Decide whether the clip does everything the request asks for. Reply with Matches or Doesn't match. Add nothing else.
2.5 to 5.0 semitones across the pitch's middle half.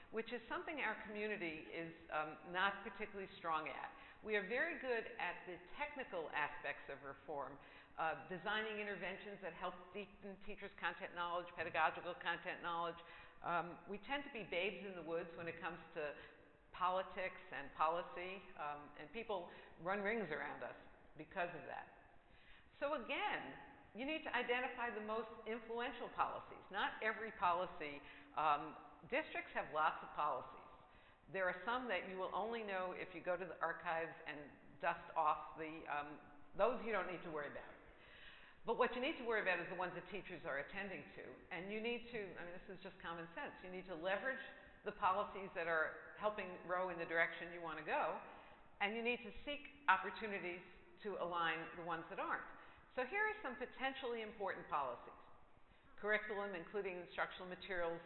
Matches